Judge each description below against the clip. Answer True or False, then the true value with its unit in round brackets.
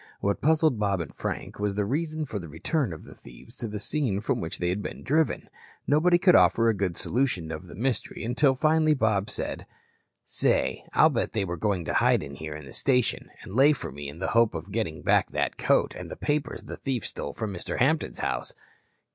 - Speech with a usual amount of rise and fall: False (8.0 semitones)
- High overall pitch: False (110 Hz)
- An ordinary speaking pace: False (220 wpm)